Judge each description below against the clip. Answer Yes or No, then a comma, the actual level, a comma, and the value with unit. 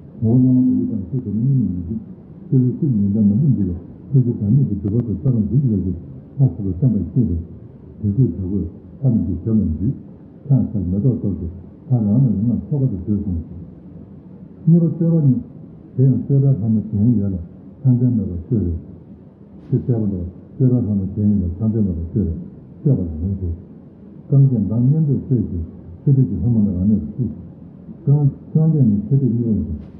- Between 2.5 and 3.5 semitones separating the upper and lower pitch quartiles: No, wide, 5.5 semitones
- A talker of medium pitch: No, low, 110 Hz